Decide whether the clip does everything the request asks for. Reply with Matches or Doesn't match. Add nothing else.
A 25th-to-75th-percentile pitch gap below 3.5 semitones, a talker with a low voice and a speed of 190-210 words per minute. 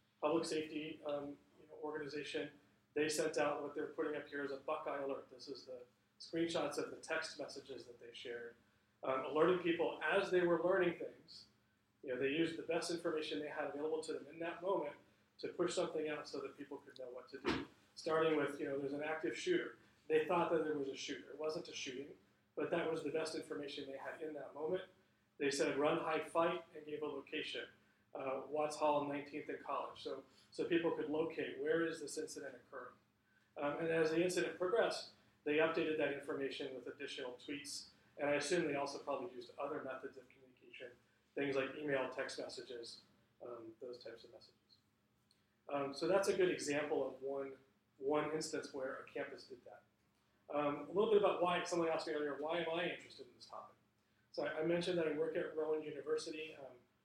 Doesn't match